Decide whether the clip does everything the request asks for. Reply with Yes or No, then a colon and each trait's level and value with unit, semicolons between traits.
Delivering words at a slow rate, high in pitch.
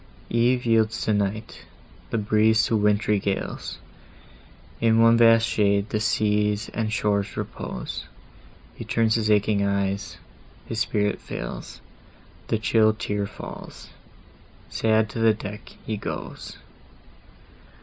No: slow, 115 wpm; low, 110 Hz